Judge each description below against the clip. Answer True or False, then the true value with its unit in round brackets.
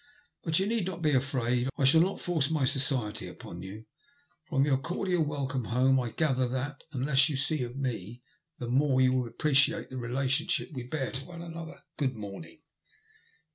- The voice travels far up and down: False (3.8 semitones)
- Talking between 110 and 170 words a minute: False (185 wpm)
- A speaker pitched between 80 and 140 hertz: True (135 Hz)